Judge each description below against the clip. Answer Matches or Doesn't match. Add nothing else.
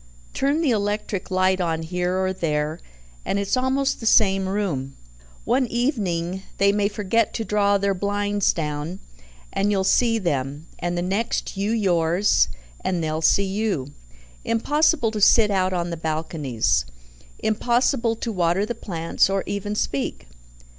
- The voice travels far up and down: Doesn't match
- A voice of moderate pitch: Doesn't match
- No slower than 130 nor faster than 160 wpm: Matches